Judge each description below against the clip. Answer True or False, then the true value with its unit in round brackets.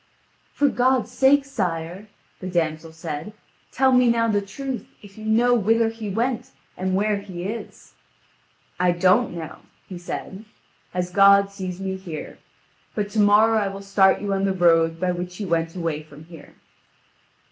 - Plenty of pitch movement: False (4.1 semitones)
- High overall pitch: True (195 Hz)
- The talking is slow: False (170 wpm)